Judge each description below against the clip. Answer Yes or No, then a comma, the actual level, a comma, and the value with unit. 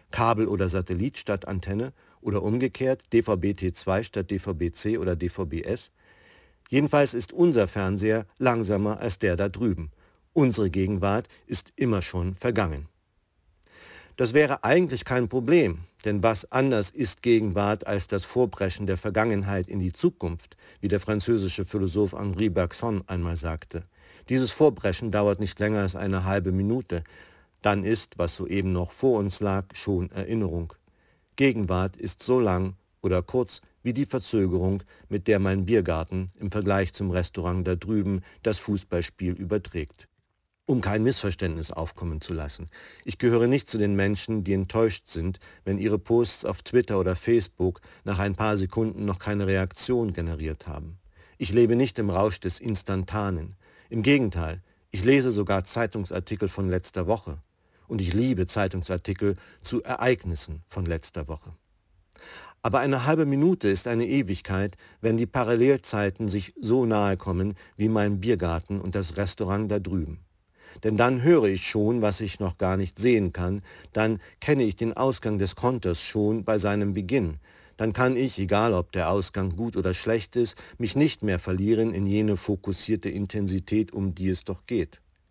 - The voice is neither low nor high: No, low, 100 Hz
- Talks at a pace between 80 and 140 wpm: No, average, 155 wpm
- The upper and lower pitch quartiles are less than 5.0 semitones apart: Yes, average, 3.5 semitones